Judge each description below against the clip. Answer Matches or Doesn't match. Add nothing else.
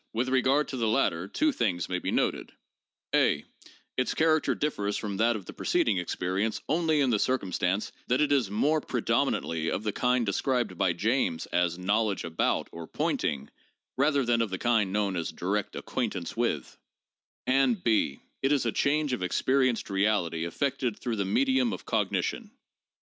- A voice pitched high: Doesn't match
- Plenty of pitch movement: Matches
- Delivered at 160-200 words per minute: Matches